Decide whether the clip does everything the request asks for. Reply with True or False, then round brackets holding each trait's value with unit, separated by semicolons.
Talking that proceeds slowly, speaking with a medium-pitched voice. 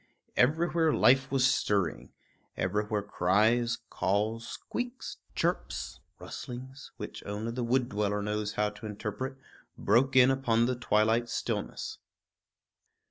False (115 wpm; 115 Hz)